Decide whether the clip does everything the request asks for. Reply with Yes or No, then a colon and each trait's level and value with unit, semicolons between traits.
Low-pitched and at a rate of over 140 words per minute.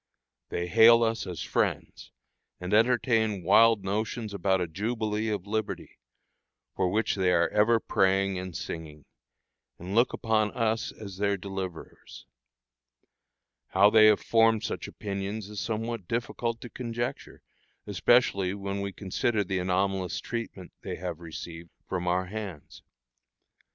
No: low, 100 Hz; slow, 135 wpm